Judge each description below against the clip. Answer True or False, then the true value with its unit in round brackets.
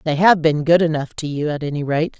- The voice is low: False (155 Hz)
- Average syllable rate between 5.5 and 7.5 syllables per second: True (5.8 syllables/s)